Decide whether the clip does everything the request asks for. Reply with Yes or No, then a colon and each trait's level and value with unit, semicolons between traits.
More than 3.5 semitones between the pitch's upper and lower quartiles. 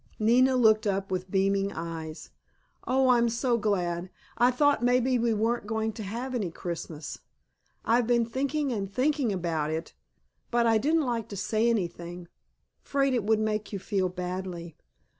Yes: average, 4.7 semitones